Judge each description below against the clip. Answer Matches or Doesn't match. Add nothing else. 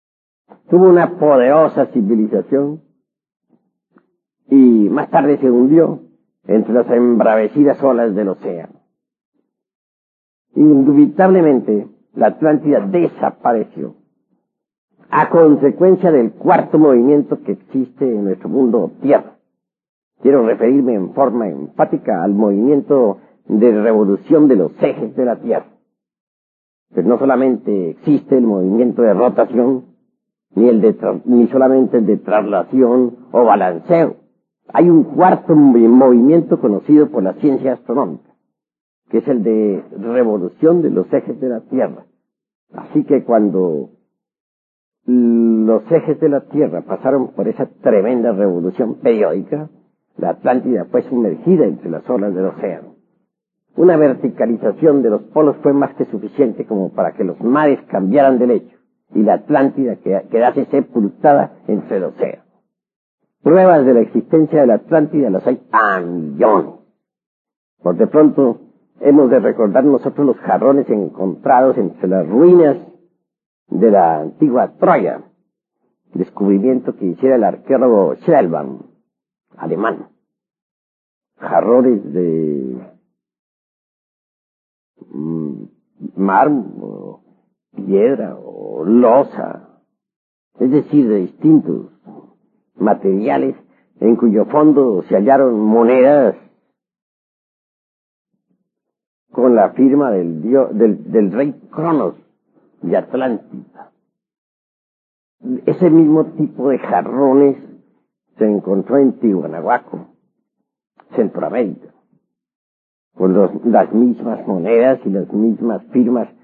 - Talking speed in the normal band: Doesn't match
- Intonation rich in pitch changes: Matches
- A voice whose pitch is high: Doesn't match